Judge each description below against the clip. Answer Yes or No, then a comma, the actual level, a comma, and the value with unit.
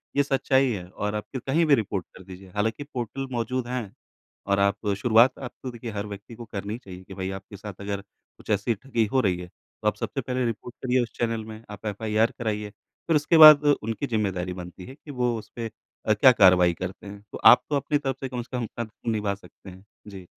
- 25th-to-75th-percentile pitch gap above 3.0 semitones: Yes, average, 4.1 semitones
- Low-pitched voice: Yes, low, 110 Hz